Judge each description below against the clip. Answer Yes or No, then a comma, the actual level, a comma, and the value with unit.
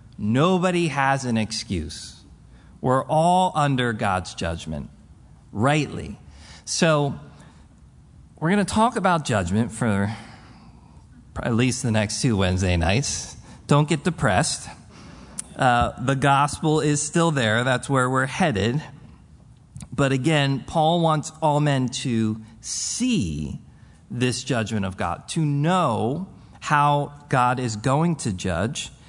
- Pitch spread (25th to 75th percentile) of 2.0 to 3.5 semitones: No, wide, 5.4 semitones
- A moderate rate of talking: No, slow, 120 wpm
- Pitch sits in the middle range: No, low, 130 Hz